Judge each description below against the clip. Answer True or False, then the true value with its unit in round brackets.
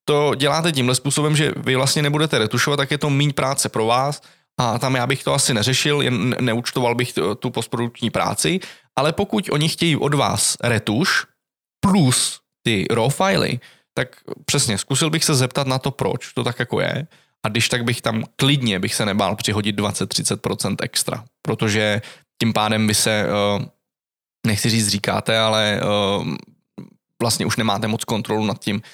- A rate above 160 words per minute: True (170 wpm)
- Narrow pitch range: False (4.6 semitones)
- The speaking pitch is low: True (125 Hz)